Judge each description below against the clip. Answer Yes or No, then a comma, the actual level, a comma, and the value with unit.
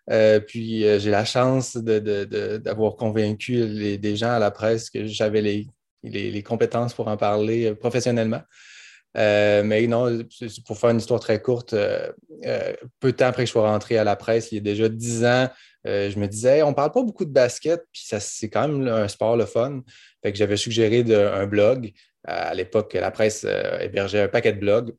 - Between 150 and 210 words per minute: No, fast, 220 wpm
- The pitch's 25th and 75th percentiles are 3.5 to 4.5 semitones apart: No, narrow, 2.6 semitones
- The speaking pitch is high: No, low, 115 Hz